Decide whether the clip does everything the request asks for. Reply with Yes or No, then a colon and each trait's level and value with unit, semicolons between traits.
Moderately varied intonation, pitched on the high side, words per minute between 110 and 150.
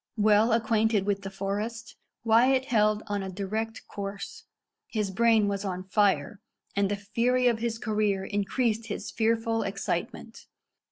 No: narrow, 2.2 semitones; high, 210 Hz; average, 145 wpm